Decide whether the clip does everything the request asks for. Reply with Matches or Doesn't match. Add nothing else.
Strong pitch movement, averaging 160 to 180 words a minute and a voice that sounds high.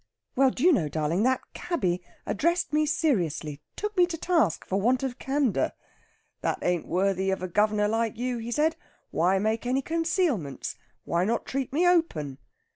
Matches